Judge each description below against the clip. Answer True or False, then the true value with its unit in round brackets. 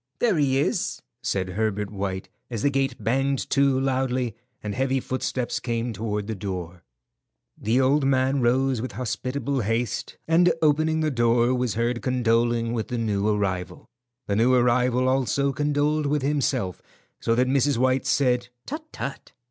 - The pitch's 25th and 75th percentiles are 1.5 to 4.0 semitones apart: True (3.2 semitones)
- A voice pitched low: True (125 Hz)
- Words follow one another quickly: False (155 wpm)